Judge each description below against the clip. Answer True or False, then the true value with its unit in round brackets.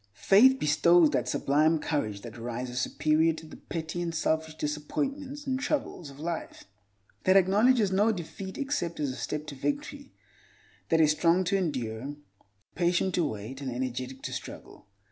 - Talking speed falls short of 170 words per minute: True (160 wpm)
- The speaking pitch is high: False (160 Hz)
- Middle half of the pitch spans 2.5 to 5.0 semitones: False (5.5 semitones)